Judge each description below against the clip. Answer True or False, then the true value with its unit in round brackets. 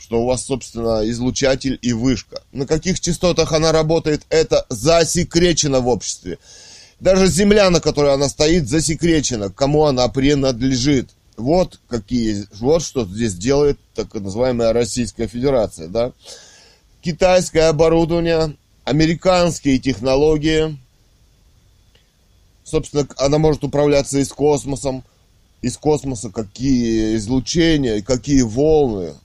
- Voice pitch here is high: False (135 Hz)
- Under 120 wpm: True (110 wpm)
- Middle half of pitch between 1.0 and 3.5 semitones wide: False (5.1 semitones)